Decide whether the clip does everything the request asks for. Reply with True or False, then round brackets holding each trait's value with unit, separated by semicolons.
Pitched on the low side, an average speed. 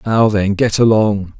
True (105 Hz; 175 wpm)